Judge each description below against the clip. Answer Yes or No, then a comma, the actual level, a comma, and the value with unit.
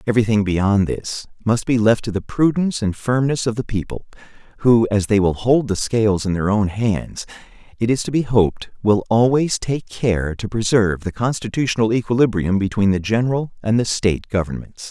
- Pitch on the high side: No, low, 110 Hz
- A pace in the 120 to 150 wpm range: No, average, 190 wpm